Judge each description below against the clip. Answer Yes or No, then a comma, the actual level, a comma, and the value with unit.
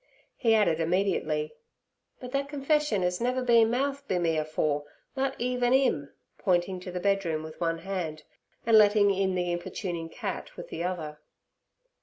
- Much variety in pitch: Yes, wide, 6.6 semitones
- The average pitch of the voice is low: No, high, 190 Hz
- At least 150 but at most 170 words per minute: Yes, average, 160 wpm